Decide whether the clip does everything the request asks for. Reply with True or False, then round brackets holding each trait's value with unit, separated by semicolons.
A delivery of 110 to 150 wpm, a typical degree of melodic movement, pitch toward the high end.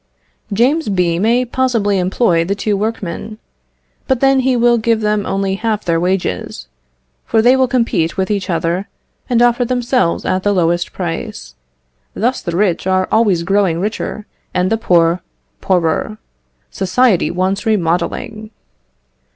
True (145 wpm; 4.5 semitones; 200 Hz)